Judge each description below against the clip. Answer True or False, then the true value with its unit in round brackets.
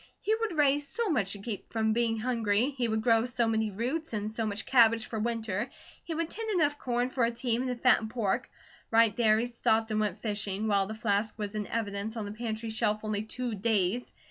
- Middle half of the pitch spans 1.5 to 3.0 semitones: True (2.4 semitones)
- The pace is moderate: False (225 wpm)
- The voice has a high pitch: True (225 Hz)